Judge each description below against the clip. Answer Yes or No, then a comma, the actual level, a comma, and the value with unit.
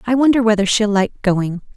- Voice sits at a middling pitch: No, high, 215 Hz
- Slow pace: No, fast, 205 wpm